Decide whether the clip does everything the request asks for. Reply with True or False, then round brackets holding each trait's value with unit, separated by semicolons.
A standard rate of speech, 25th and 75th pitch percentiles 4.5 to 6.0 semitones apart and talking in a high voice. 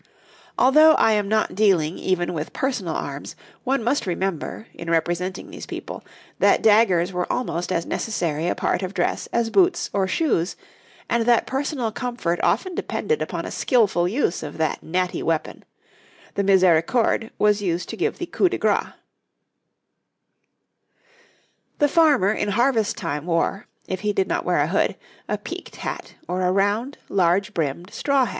True (165 wpm; 5.6 semitones; 200 Hz)